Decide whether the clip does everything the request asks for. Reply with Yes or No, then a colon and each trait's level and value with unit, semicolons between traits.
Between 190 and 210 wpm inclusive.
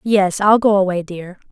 Yes: average, 200 wpm